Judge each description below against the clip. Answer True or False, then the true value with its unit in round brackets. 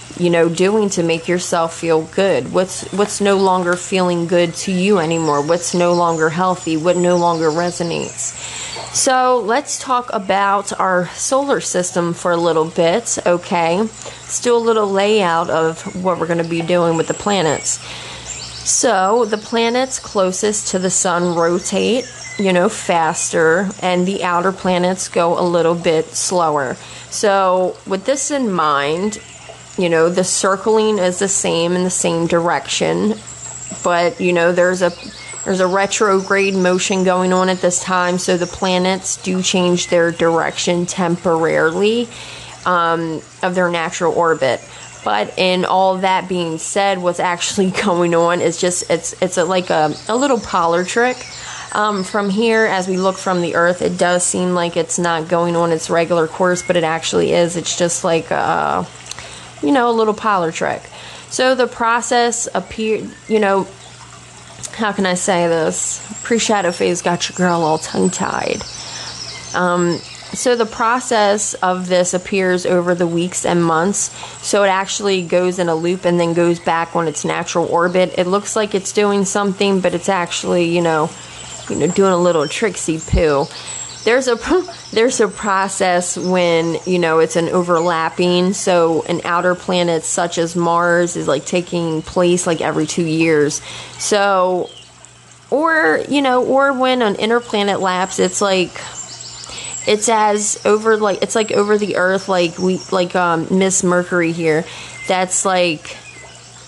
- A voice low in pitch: False (180 Hz)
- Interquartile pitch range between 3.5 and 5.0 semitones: False (2.7 semitones)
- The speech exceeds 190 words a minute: False (160 wpm)